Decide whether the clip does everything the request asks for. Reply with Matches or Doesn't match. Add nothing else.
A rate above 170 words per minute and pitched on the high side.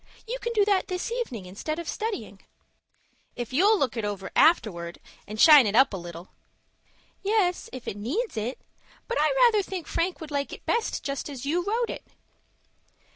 Matches